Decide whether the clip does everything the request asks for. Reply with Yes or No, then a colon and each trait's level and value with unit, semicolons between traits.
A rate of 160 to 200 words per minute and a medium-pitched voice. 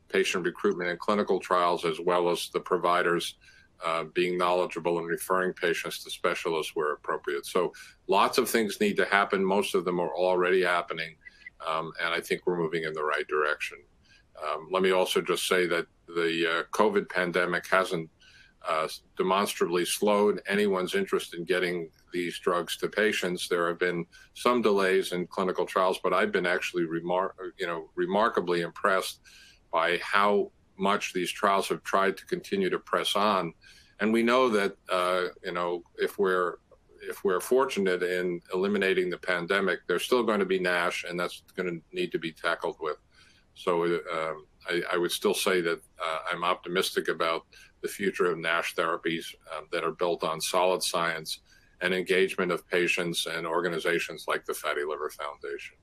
No: average, 175 wpm; very low, 90 Hz